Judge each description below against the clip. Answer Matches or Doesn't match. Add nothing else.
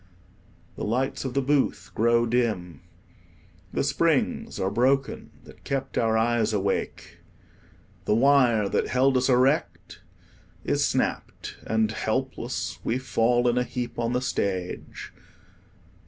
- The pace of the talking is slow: Matches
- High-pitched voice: Doesn't match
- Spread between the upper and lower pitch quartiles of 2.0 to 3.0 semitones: Matches